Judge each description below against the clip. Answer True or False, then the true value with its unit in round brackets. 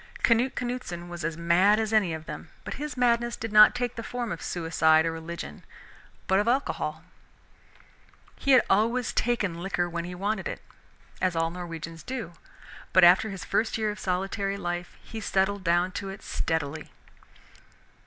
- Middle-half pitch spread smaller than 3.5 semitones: False (4.6 semitones)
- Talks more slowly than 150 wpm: False (170 wpm)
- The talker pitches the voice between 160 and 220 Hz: True (190 Hz)